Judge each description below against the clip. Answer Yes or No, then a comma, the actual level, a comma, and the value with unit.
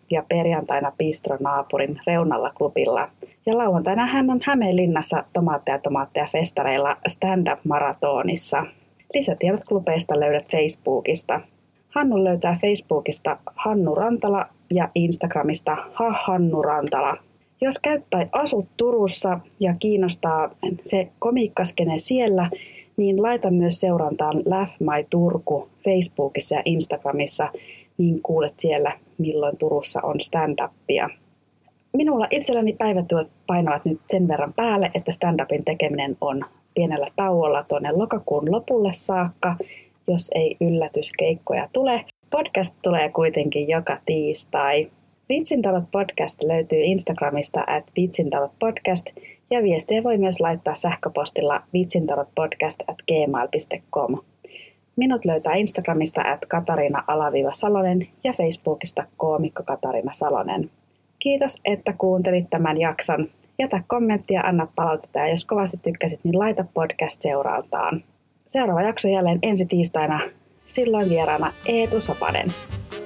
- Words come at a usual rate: Yes, average, 110 wpm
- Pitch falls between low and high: Yes, medium, 175 Hz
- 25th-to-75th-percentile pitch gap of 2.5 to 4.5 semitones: No, average, 5.0 semitones